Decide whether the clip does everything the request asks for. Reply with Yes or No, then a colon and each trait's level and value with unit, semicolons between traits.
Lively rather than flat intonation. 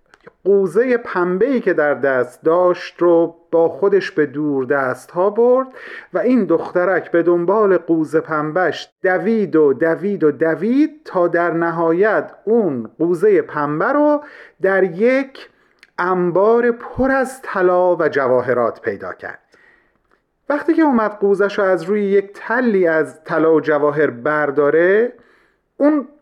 Yes: wide, 6.3 semitones